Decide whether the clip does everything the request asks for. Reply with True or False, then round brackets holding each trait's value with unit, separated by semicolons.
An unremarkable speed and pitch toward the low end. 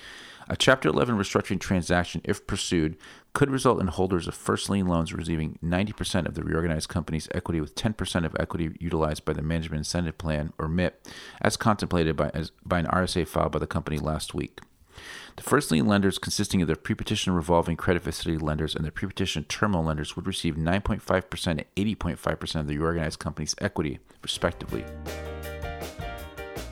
True (170 wpm; 85 Hz)